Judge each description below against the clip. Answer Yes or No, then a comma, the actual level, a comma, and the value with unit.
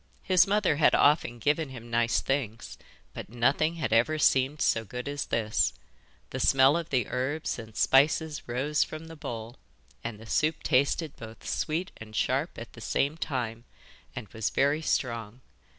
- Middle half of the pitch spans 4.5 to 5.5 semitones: Yes, average, 4.8 semitones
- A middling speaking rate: Yes, average, 165 wpm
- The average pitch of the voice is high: No, low, 135 Hz